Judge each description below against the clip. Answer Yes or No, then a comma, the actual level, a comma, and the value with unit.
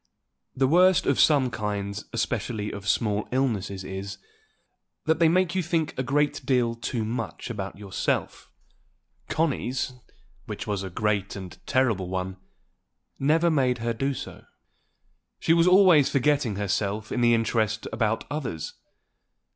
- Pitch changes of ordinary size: No, wide, 5.9 semitones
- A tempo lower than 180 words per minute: Yes, average, 140 wpm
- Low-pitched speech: Yes, low, 115 Hz